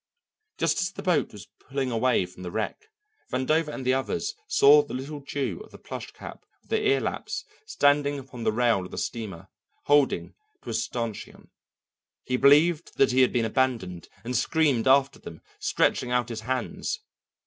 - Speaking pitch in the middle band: No, low, 130 Hz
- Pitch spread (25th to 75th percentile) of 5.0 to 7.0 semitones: No, average, 4.2 semitones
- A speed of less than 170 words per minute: No, average, 180 wpm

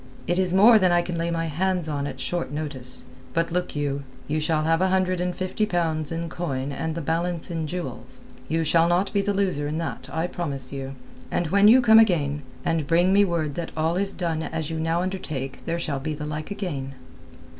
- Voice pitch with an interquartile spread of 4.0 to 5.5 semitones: No, average, 3.1 semitones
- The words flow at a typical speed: No, fast, 220 wpm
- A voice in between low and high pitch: Yes, medium, 165 Hz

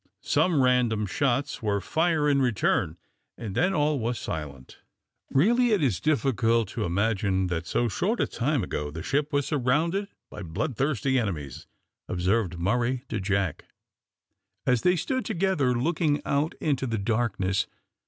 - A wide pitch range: Yes, wide, 6.9 semitones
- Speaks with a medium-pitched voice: No, low, 125 Hz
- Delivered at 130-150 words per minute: Yes, average, 145 wpm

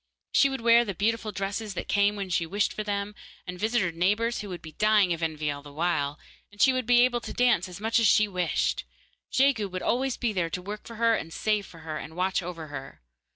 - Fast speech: Yes, fast, 245 wpm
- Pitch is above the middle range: Yes, high, 200 Hz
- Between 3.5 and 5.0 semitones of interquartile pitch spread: Yes, average, 4.7 semitones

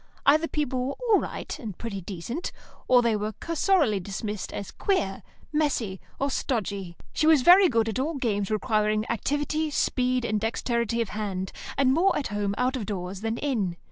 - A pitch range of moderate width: No, wide, 5.7 semitones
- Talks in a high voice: Yes, high, 235 Hz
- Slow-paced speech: No, average, 175 wpm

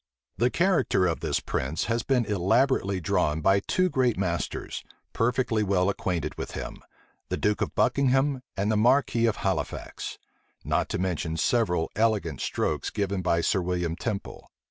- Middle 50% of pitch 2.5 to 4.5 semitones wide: No, average, 5.2 semitones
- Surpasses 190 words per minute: No, average, 155 wpm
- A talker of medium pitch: No, low, 100 Hz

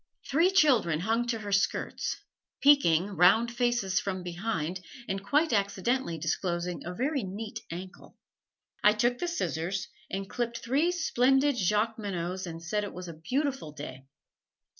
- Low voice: No, high, 205 Hz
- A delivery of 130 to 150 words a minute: Yes, average, 140 wpm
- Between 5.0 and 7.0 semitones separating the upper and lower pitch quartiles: Yes, wide, 5.5 semitones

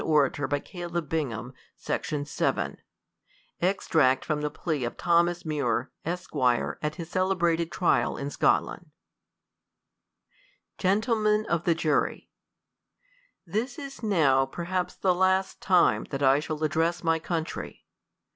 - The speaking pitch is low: No, medium, 165 Hz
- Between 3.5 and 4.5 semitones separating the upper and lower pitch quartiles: Yes, average, 3.8 semitones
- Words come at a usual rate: No, slow, 120 wpm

